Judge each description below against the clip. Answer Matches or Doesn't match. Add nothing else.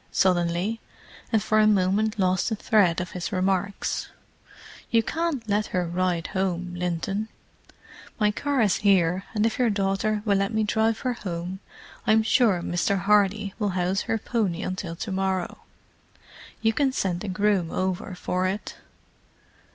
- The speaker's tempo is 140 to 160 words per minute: Matches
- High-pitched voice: Matches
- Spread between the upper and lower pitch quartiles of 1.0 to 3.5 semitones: Matches